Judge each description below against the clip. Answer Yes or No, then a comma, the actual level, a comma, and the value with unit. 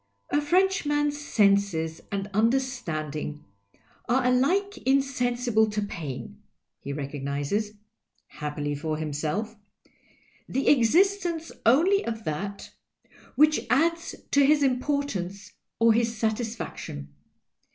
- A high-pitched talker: Yes, high, 230 Hz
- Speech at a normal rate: No, slow, 110 wpm